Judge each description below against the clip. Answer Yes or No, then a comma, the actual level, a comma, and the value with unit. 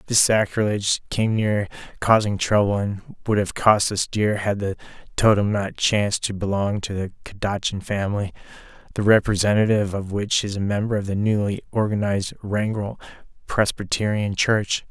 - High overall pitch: No, low, 100 Hz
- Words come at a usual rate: Yes, average, 150 wpm